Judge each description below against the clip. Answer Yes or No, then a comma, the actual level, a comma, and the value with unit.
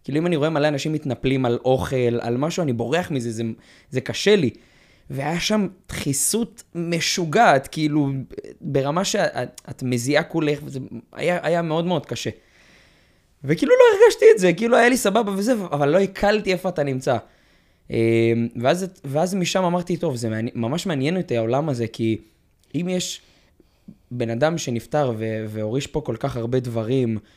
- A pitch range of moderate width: No, wide, 6.8 semitones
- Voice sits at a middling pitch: Yes, medium, 145 Hz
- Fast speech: Yes, fast, 160 wpm